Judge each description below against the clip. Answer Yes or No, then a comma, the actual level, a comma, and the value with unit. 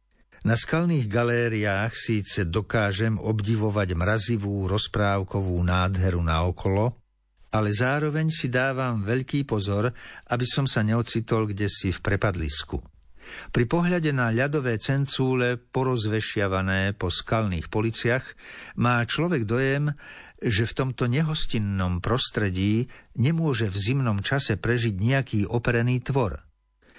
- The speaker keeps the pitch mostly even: No, average, 4.0 semitones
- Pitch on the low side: Yes, low, 115 Hz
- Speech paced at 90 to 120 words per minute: Yes, slow, 110 wpm